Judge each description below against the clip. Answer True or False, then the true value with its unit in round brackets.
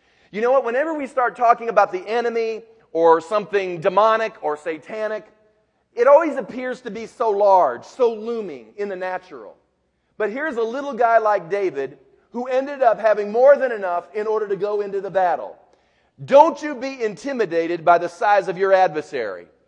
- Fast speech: False (175 wpm)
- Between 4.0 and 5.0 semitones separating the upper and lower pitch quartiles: True (4.6 semitones)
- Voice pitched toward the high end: True (220 Hz)